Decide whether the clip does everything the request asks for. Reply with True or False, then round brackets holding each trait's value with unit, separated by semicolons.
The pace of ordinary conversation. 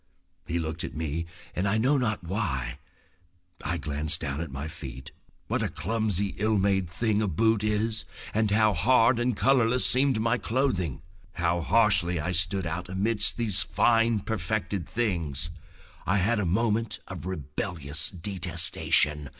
True (150 wpm)